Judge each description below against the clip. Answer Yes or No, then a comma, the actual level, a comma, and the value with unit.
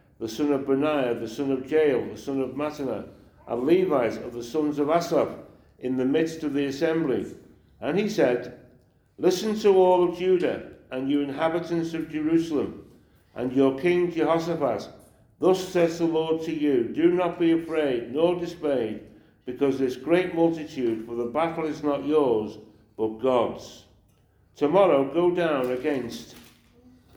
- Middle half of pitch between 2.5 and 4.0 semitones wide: No, average, 4.8 semitones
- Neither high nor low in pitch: Yes, medium, 150 Hz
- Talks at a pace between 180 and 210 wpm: No, average, 155 wpm